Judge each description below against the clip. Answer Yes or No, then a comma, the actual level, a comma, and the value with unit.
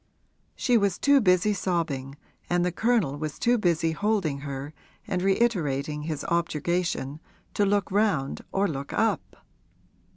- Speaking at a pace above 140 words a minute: No, slow, 135 wpm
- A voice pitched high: No, medium, 175 Hz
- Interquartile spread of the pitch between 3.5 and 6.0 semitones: Yes, wide, 5.4 semitones